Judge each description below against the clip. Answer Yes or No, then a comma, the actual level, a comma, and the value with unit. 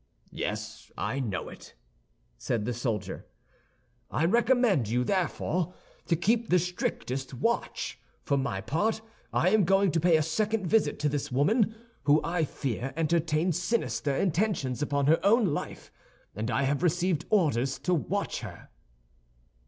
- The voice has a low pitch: No, medium, 165 Hz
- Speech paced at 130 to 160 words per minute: Yes, average, 145 wpm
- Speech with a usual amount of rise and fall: No, wide, 5.9 semitones